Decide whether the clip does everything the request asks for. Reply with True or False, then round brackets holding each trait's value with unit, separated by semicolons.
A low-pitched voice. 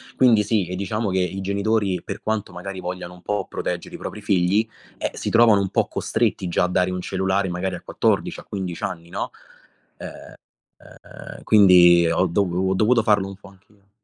True (95 Hz)